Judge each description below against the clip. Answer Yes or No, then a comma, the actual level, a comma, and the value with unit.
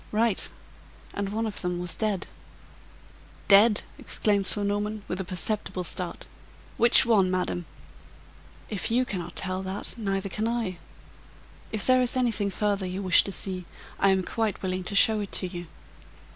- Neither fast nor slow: Yes, average, 160 wpm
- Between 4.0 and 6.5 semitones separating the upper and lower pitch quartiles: No, average, 2.7 semitones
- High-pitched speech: Yes, high, 200 Hz